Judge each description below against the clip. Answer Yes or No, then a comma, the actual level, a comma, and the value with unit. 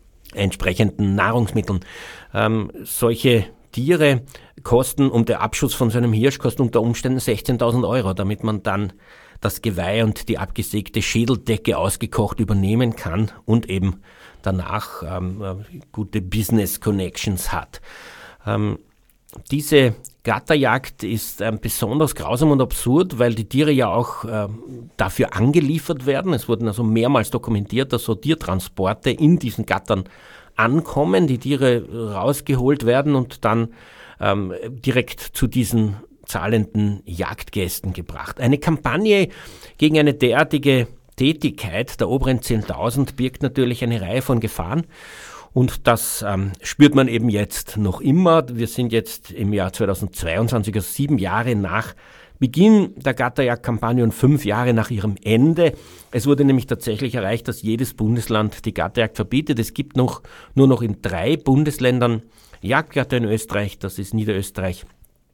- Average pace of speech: Yes, average, 135 wpm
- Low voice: Yes, low, 115 Hz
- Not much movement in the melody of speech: No, average, 3.8 semitones